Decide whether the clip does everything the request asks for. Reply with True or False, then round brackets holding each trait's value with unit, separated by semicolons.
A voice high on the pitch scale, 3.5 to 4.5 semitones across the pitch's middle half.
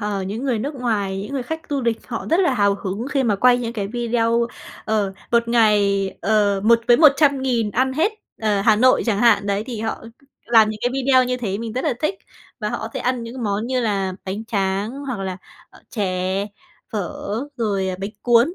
True (225 Hz; 3.8 semitones)